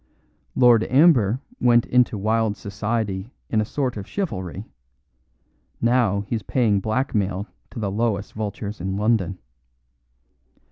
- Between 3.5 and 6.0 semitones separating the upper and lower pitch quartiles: No, average, 3.0 semitones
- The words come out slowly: Yes, slow, 120 wpm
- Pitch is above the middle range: No, low, 110 Hz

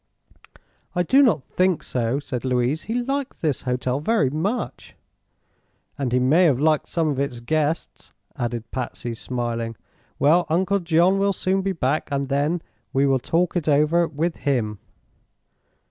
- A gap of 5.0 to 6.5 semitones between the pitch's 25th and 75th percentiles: Yes, wide, 5.5 semitones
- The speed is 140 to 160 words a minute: Yes, average, 155 wpm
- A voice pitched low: No, medium, 150 Hz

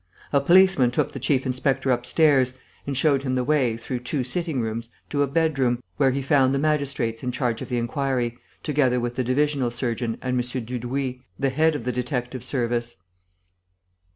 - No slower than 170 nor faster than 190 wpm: Yes, average, 180 wpm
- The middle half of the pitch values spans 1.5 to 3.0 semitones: Yes, narrow, 2.5 semitones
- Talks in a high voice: No, low, 130 Hz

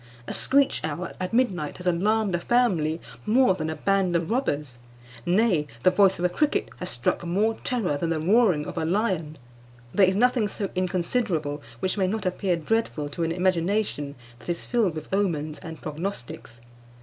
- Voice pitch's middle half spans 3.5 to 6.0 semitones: Yes, average, 4.8 semitones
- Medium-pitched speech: Yes, medium, 180 Hz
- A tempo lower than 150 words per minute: No, average, 180 wpm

